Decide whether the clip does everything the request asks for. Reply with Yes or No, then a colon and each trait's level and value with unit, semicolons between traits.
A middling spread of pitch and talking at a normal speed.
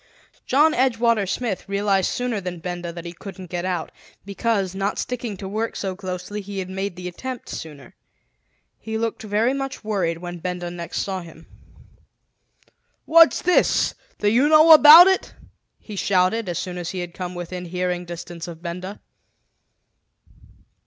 Yes: average, 4.2 semitones; average, 160 wpm